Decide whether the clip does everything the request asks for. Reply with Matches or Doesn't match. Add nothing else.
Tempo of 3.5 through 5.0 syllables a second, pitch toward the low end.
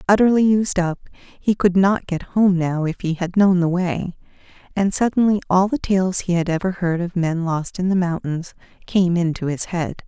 Doesn't match